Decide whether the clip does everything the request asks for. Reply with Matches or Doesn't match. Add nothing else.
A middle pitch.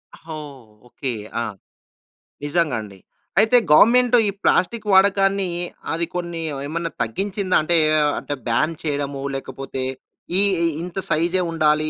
Matches